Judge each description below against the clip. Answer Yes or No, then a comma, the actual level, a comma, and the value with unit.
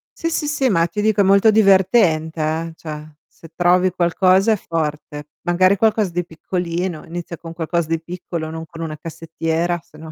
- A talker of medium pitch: Yes, medium, 170 Hz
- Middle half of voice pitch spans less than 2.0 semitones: No, average, 2.7 semitones